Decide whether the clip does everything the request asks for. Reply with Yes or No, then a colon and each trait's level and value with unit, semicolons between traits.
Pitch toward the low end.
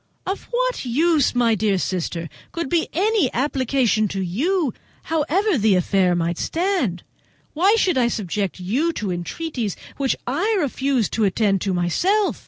No: very high, 250 Hz